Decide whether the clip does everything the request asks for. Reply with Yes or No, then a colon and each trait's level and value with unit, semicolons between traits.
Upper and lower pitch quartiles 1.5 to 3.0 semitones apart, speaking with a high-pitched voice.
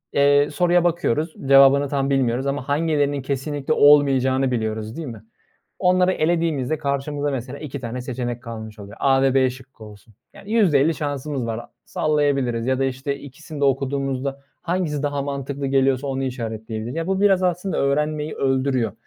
No: narrow, 2.5 semitones; medium, 140 Hz